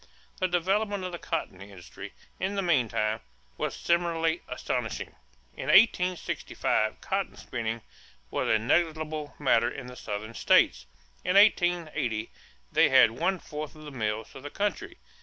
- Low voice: No, medium, 155 Hz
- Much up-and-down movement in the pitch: Yes, wide, 7.7 semitones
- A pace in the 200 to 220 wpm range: No, average, 140 wpm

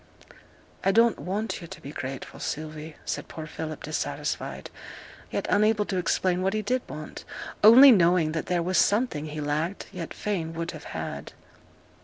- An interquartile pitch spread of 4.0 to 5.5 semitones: Yes, average, 4.9 semitones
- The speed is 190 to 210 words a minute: No, average, 165 wpm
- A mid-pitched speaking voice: Yes, medium, 175 Hz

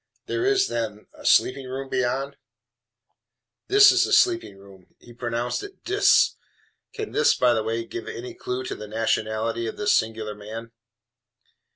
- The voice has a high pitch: No, low, 120 Hz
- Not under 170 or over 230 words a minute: No, average, 160 wpm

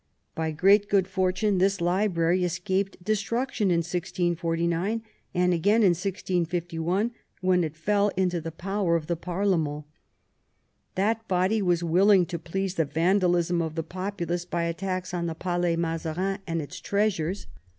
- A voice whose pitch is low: No, medium, 180 Hz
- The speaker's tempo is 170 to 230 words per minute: No, average, 145 wpm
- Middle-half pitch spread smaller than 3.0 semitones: Yes, narrow, 2.6 semitones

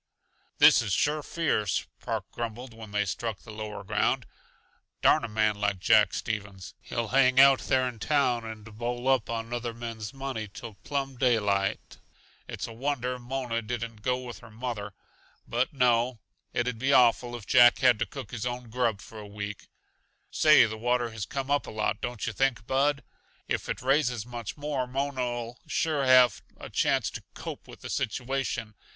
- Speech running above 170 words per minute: Yes, average, 180 wpm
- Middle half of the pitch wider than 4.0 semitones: No, average, 2.9 semitones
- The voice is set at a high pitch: No, low, 120 Hz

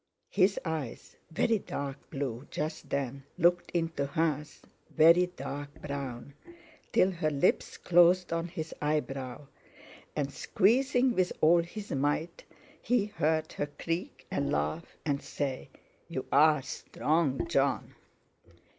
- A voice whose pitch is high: No, medium, 155 Hz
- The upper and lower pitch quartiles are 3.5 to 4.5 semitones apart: Yes, average, 3.8 semitones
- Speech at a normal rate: No, slow, 120 wpm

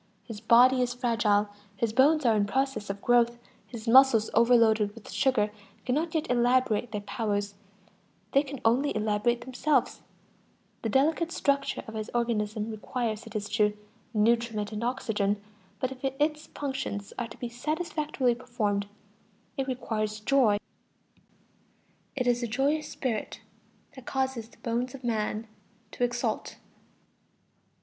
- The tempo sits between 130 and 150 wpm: Yes, average, 140 wpm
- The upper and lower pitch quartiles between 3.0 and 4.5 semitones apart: Yes, average, 3.5 semitones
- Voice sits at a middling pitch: No, high, 235 Hz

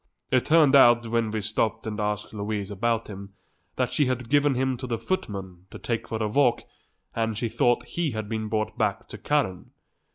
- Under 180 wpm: No, average, 200 wpm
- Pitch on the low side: Yes, low, 115 Hz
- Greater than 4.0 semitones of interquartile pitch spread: No, average, 3.3 semitones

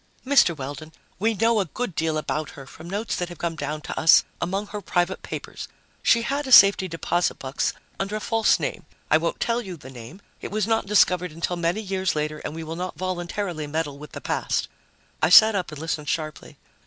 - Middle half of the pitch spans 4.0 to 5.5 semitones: Yes, average, 4.8 semitones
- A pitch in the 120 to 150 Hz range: No, medium, 175 Hz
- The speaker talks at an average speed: No, fast, 215 wpm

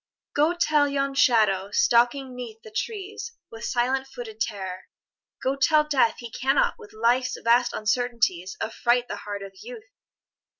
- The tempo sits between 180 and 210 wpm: No, average, 145 wpm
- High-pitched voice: Yes, high, 245 Hz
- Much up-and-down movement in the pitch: No, average, 4.1 semitones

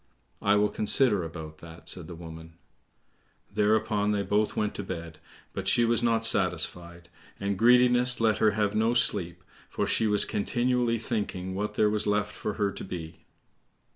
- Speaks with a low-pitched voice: Yes, low, 105 Hz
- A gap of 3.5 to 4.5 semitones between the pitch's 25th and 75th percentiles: Yes, average, 3.8 semitones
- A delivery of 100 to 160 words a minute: No, average, 170 wpm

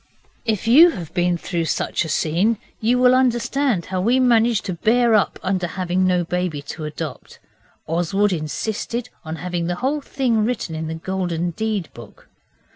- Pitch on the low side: No, medium, 185 Hz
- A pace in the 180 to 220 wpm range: No, average, 170 wpm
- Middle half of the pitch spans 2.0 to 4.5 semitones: No, wide, 5.4 semitones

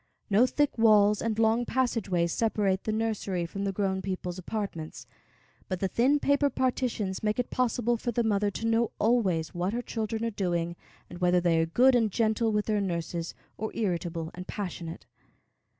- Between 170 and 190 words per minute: Yes, average, 180 wpm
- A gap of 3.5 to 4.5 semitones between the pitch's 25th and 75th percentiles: Yes, average, 4.0 semitones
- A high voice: Yes, high, 210 Hz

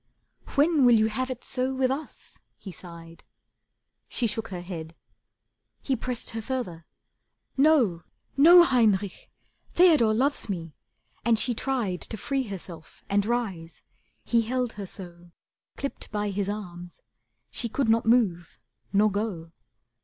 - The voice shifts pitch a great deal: Yes, wide, 5.9 semitones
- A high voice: Yes, high, 220 Hz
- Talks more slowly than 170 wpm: Yes, average, 140 wpm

